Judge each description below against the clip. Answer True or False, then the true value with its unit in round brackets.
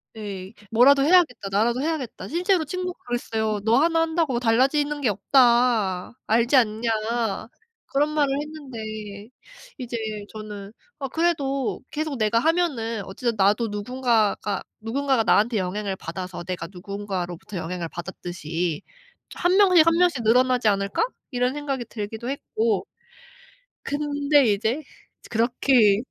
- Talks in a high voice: True (235 Hz)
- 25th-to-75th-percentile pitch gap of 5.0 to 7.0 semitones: True (5.5 semitones)